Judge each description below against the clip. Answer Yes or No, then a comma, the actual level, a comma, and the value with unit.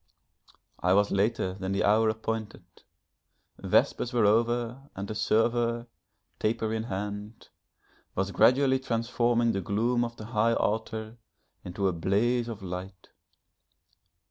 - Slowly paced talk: Yes, slow, 125 wpm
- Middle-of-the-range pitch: No, low, 110 Hz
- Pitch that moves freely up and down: No, average, 2.8 semitones